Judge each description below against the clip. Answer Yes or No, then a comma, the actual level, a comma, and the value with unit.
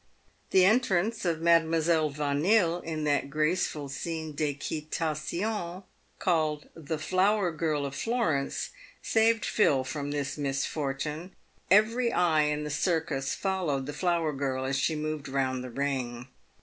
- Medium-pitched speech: Yes, medium, 155 Hz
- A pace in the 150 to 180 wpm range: No, slow, 135 wpm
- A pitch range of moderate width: Yes, average, 3.7 semitones